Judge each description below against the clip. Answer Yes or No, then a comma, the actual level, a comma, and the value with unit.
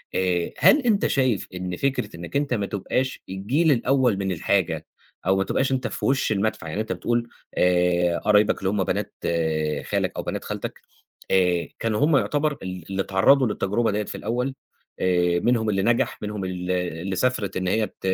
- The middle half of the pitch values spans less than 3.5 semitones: No, average, 5.1 semitones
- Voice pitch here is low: Yes, low, 100 Hz